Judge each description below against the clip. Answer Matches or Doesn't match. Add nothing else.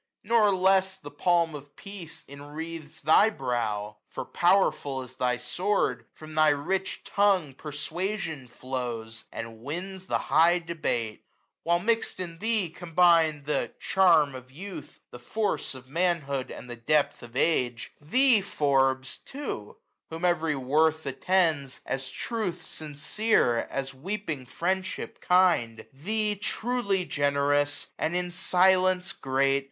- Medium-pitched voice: Matches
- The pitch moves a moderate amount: Doesn't match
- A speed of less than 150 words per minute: Matches